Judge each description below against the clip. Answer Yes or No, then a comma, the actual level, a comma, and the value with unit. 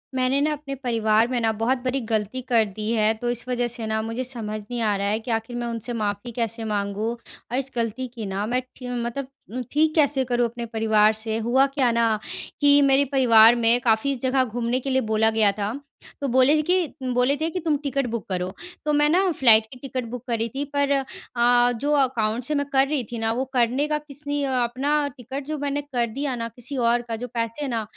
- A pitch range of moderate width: Yes, average, 3.5 semitones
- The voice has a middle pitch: No, high, 245 Hz